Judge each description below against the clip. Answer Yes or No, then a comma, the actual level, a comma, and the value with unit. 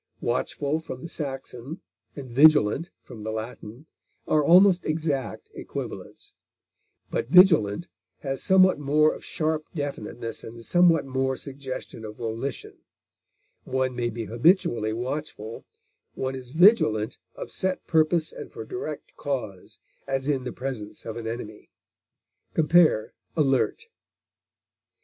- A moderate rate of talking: No, slow, 120 wpm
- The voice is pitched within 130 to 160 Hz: Yes, low, 135 Hz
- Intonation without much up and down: No, average, 5.1 semitones